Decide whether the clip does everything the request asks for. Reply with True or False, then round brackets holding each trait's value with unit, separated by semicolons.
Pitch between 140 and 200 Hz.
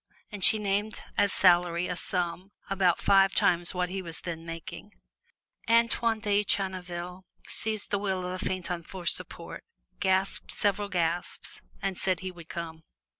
True (185 Hz)